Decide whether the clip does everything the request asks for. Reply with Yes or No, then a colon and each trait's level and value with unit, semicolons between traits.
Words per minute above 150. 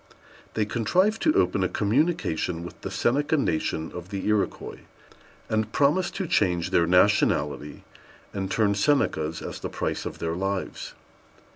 No: average, 145 wpm